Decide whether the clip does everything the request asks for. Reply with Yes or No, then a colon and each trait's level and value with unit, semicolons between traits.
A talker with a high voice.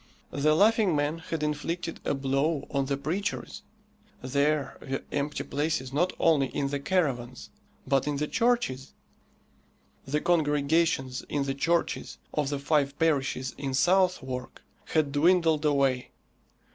No: medium, 145 Hz